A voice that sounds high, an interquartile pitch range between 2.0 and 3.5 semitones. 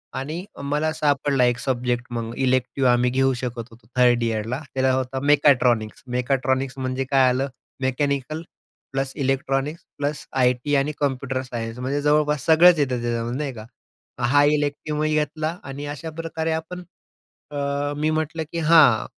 No: low, 135 Hz; average, 2.9 semitones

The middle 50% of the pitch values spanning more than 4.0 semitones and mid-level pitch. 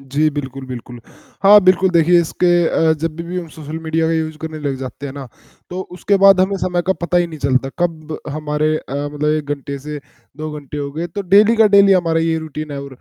No: average, 3.4 semitones; medium, 155 Hz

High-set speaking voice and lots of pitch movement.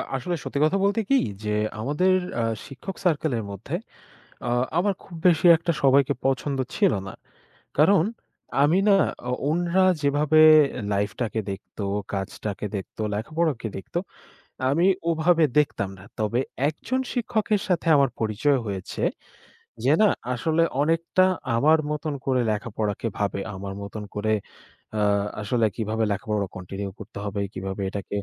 No: low, 135 Hz; wide, 8.0 semitones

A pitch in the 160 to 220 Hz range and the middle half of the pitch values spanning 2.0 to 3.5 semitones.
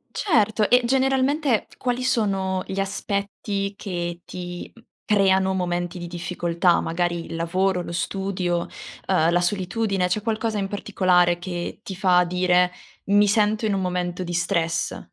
Yes: high, 190 Hz; average, 2.7 semitones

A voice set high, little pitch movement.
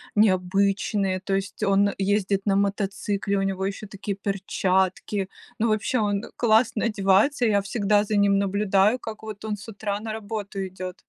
Yes: high, 200 Hz; narrow, 1.5 semitones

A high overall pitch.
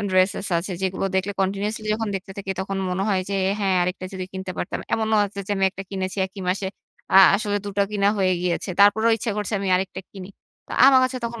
Yes: high, 195 Hz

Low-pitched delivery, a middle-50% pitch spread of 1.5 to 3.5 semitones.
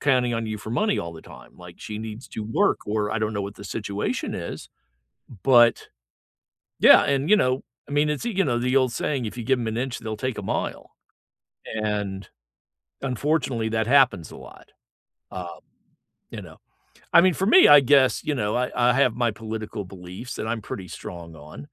No: low, 115 Hz; average, 4.1 semitones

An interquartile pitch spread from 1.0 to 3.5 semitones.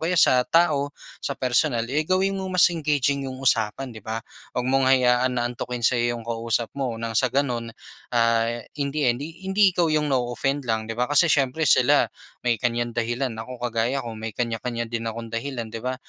Yes: average, 3.2 semitones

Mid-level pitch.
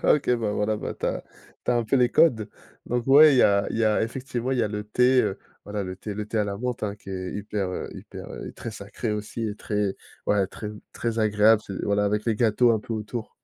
No: low, 105 Hz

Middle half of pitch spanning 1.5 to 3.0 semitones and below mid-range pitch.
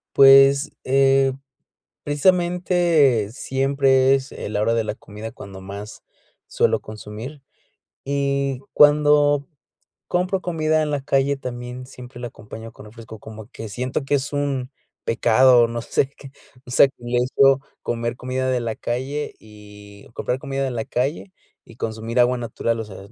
No: average, 3.4 semitones; low, 130 Hz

